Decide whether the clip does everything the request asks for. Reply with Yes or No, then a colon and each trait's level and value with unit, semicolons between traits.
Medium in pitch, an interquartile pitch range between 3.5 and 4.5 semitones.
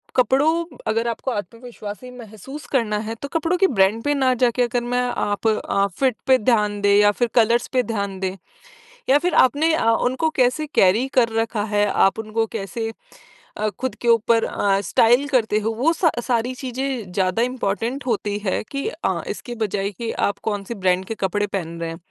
No: high, 230 Hz; average, 3.9 semitones